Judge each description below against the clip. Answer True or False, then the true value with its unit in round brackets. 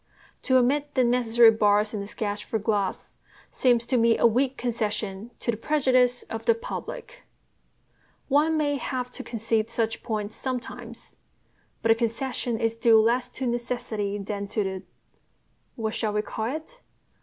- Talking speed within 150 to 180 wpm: True (160 wpm)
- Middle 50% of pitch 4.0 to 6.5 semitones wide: False (2.9 semitones)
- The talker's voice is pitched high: True (235 Hz)